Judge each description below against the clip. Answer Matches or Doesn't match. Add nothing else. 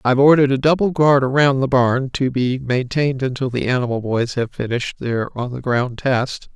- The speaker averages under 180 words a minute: Doesn't match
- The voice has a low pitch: Matches